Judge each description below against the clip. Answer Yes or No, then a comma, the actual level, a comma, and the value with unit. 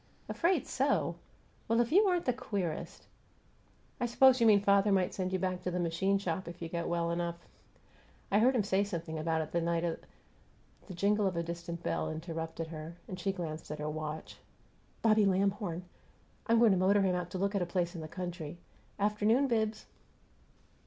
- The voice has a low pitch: No, medium, 185 Hz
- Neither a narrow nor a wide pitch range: Yes, average, 3.5 semitones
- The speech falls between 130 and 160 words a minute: No, average, 200 wpm